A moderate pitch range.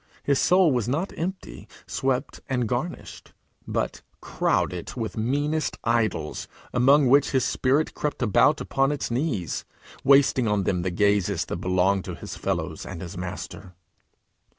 No: wide, 6.3 semitones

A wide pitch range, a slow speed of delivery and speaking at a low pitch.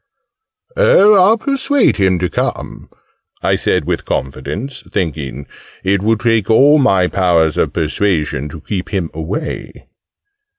Yes: wide, 8.8 semitones; slow, 130 wpm; very low, 95 Hz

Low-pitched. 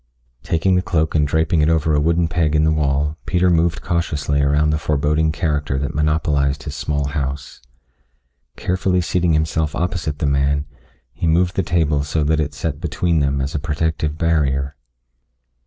Yes: very low, 75 Hz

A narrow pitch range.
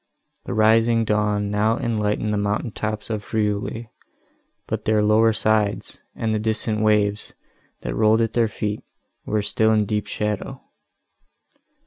Yes: narrow, 1.0 semitones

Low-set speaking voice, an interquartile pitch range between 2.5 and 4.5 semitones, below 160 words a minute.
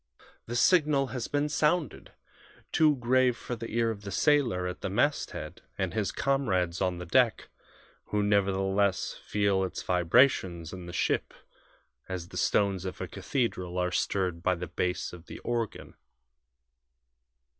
No: low, 100 Hz; wide, 5.5 semitones; average, 150 wpm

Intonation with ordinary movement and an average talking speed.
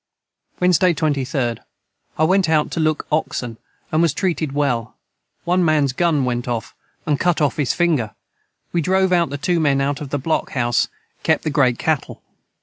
Yes: average, 4.0 semitones; average, 175 wpm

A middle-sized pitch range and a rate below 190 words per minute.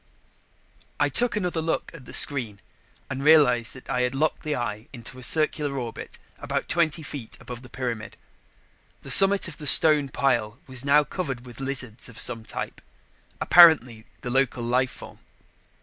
Yes: average, 4.1 semitones; average, 165 wpm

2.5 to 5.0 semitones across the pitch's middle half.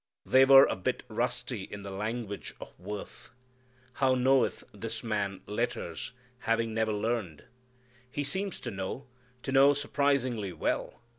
Yes: average, 4.7 semitones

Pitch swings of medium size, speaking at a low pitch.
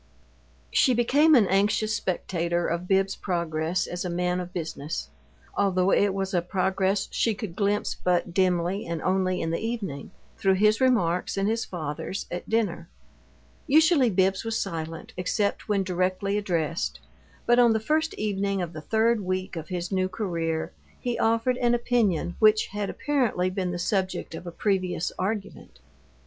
No: average, 3.4 semitones; high, 190 Hz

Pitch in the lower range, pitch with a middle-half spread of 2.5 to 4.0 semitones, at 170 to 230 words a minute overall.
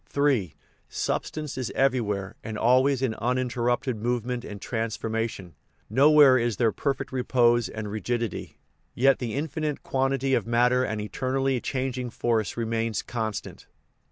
No: low, 120 Hz; average, 2.8 semitones; average, 140 wpm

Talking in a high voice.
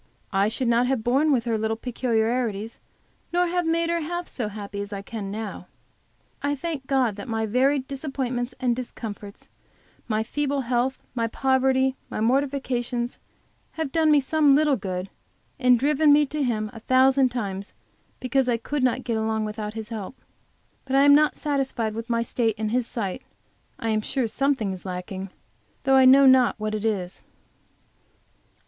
Yes: high, 245 Hz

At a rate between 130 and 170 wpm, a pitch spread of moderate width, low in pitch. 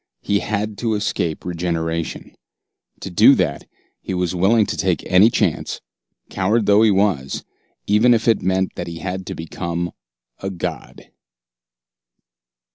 Yes: average, 140 wpm; average, 3.4 semitones; very low, 95 Hz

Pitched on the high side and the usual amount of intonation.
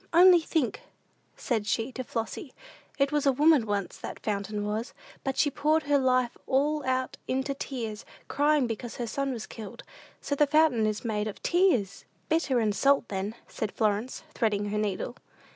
Yes: very high, 255 Hz; average, 5.0 semitones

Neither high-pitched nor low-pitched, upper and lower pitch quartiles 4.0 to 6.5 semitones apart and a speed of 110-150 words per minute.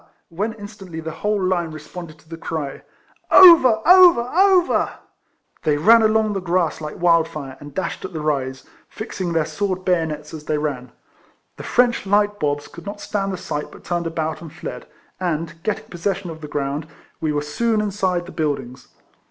No: medium, 170 Hz; average, 5.1 semitones; average, 185 wpm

